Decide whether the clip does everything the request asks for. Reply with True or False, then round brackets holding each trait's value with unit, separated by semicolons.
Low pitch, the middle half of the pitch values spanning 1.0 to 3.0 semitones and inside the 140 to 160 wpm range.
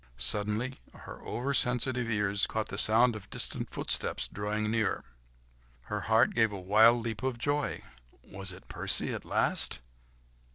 True (110 Hz; 2.7 semitones; 150 wpm)